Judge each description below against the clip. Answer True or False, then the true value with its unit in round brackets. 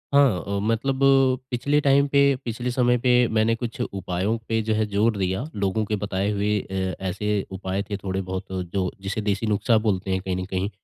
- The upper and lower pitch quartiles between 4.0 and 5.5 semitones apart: False (3.2 semitones)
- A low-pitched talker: True (105 Hz)